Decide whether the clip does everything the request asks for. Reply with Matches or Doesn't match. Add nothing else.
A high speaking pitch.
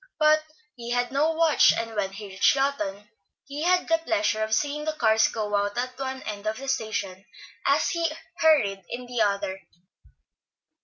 Matches